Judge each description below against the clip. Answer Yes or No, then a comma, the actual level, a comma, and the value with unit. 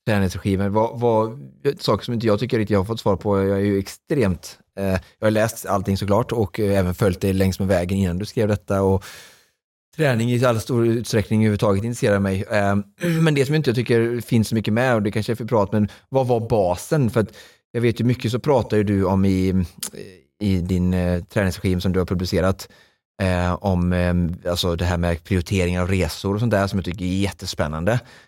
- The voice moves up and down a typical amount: Yes, average, 3.4 semitones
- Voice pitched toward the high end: No, low, 100 Hz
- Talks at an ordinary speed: No, fast, 220 wpm